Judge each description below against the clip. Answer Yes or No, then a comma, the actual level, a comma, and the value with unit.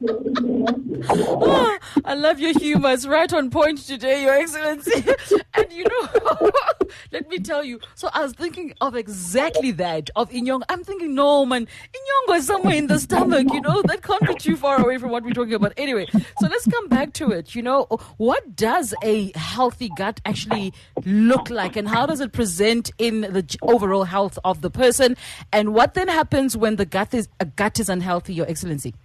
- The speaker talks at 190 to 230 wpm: Yes, average, 195 wpm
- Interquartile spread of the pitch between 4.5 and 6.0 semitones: Yes, wide, 5.6 semitones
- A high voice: Yes, high, 245 Hz